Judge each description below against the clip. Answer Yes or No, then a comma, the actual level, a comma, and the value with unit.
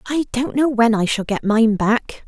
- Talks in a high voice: Yes, high, 235 Hz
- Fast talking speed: Yes, fast, 240 wpm